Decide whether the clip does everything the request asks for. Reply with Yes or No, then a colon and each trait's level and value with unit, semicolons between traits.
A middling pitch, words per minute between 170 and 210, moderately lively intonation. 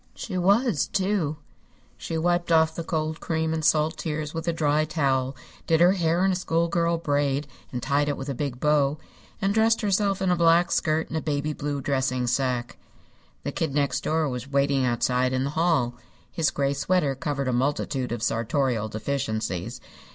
Yes: medium, 150 Hz; average, 185 wpm; average, 3.8 semitones